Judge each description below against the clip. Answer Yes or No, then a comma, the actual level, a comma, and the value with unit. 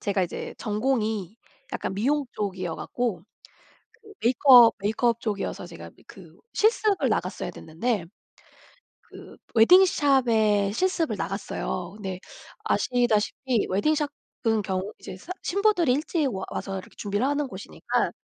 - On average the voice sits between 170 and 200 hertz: No, high, 225 Hz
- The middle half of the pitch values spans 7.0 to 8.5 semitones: No, wide, 6.3 semitones